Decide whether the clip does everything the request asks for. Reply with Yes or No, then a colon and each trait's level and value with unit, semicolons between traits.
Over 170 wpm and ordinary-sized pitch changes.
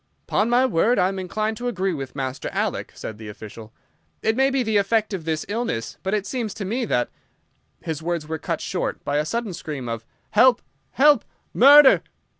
No: average, 200 wpm; wide, 7.5 semitones